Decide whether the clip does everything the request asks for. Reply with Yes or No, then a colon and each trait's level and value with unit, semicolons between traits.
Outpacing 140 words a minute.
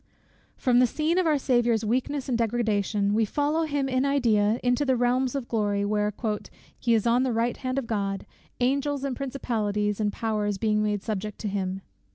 Yes: average, 190 wpm